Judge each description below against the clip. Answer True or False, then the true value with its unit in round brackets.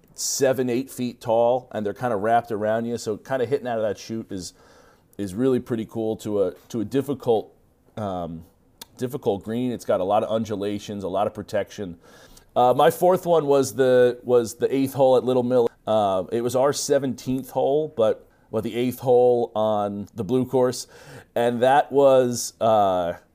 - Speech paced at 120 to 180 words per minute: False (200 wpm)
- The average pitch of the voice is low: True (120 Hz)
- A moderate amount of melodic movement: True (3.0 semitones)